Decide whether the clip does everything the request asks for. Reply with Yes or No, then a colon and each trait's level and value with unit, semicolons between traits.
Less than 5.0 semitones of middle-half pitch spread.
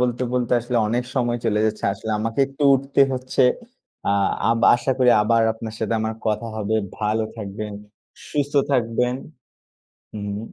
Yes: narrow, 2.4 semitones